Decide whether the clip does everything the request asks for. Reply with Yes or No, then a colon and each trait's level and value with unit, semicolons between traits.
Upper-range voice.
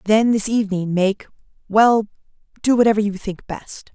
Yes: high, 210 Hz